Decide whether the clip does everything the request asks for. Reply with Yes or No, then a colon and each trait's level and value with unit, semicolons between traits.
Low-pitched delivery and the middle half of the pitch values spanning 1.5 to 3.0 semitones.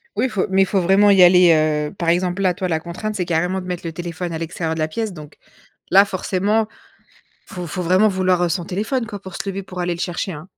No: medium, 180 Hz; narrow, 2.4 semitones